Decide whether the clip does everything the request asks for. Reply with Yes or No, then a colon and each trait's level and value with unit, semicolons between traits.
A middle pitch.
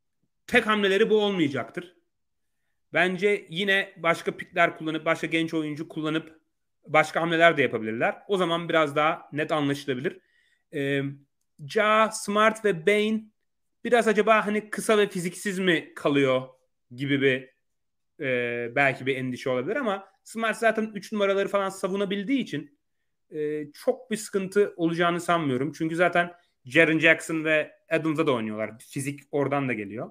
Yes: medium, 165 Hz